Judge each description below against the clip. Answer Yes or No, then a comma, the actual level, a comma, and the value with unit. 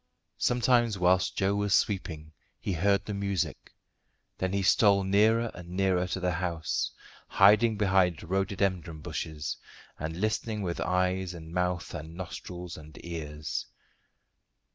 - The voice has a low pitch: Yes, very low, 95 Hz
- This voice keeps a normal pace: No, slow, 130 wpm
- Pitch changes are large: No, narrow, 2.6 semitones